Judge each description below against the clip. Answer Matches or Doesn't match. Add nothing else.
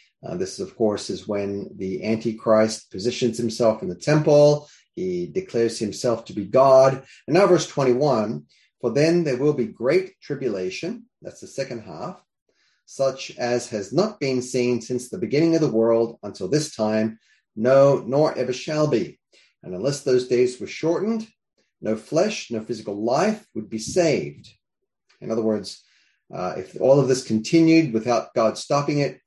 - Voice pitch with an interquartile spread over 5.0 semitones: Matches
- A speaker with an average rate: Matches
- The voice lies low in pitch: Matches